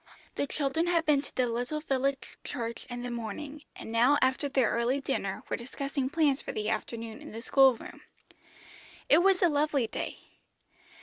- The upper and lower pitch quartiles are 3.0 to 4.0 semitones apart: Yes, average, 3.6 semitones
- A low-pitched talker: No, very high, 270 Hz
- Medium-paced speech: Yes, average, 180 wpm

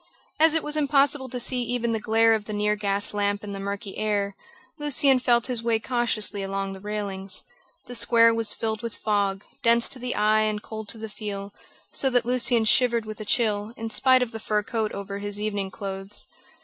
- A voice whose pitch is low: No, high, 220 Hz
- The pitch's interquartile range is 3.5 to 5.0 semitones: No, average, 2.7 semitones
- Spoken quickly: Yes, fast, 210 wpm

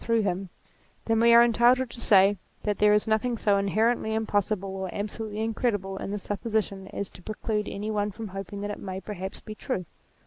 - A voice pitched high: Yes, high, 210 Hz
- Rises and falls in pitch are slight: Yes, narrow, 2.1 semitones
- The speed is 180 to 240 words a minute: Yes, fast, 205 wpm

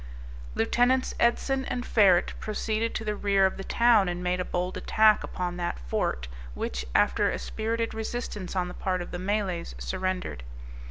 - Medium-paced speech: Yes, average, 170 wpm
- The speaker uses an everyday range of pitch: Yes, average, 3.8 semitones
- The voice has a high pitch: Yes, high, 195 Hz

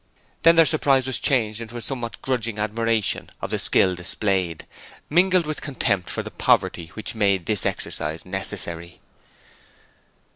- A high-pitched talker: No, low, 110 Hz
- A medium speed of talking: Yes, average, 145 wpm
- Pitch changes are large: Yes, wide, 5.7 semitones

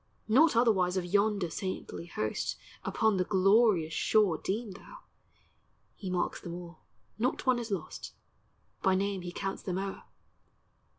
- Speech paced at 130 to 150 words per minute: Yes, average, 140 wpm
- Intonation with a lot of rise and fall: No, average, 3.4 semitones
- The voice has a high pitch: Yes, high, 195 Hz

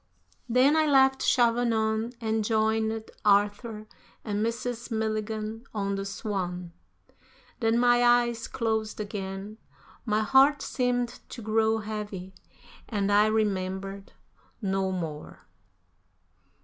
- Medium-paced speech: No, slow, 105 wpm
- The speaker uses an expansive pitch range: No, narrow, 2.5 semitones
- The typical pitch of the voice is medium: No, high, 220 Hz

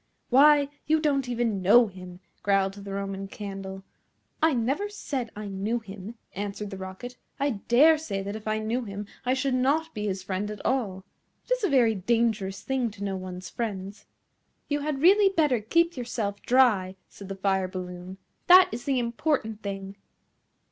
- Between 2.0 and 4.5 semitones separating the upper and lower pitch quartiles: No, average, 5.3 semitones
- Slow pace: No, average, 175 wpm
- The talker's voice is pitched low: No, high, 215 Hz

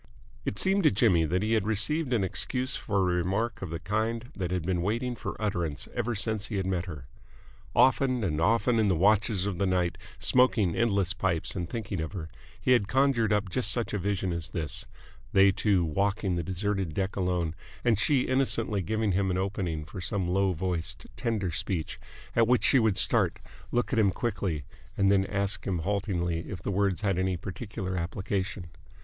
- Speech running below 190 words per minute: No, average, 195 wpm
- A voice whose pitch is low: Yes, low, 100 Hz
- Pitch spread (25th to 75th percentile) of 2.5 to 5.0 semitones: Yes, average, 3.5 semitones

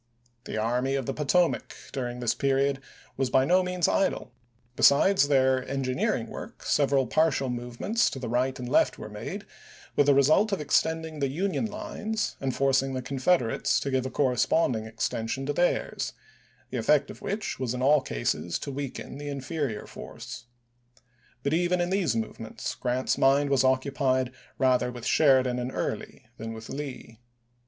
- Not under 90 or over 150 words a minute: No, average, 165 wpm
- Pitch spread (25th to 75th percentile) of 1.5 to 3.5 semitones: Yes, average, 2.9 semitones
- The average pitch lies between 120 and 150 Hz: Yes, low, 135 Hz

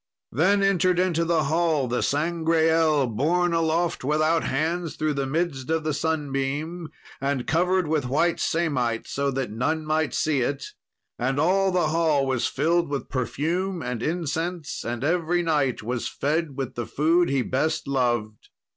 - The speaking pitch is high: No, medium, 155 Hz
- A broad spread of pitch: No, average, 3.7 semitones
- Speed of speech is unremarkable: Yes, average, 155 wpm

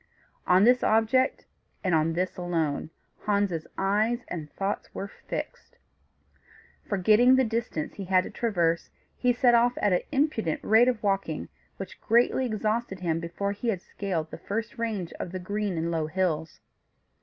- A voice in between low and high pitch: No, high, 200 Hz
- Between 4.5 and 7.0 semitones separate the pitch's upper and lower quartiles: Yes, average, 4.8 semitones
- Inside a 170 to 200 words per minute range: No, average, 160 wpm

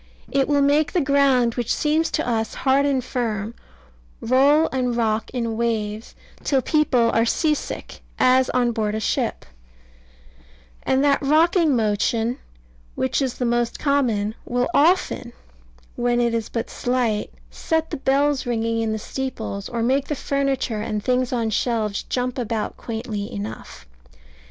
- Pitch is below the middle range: No, high, 245 Hz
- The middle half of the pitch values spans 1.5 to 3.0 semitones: No, average, 3.5 semitones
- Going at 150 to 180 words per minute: Yes, average, 155 wpm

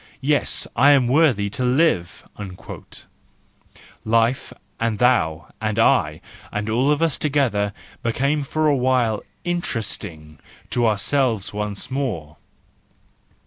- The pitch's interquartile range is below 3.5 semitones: No, average, 4.9 semitones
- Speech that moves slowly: Yes, slow, 115 wpm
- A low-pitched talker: Yes, low, 120 Hz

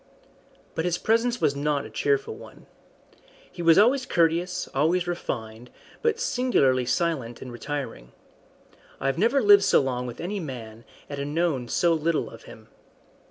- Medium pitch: Yes, medium, 155 Hz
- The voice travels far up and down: Yes, wide, 5.9 semitones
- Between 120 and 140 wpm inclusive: No, average, 155 wpm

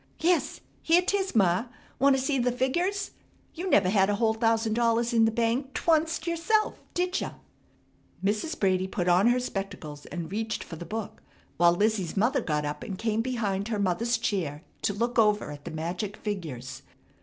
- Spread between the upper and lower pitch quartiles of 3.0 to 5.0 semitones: No, wide, 5.4 semitones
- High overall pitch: Yes, high, 220 Hz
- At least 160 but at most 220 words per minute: Yes, average, 180 wpm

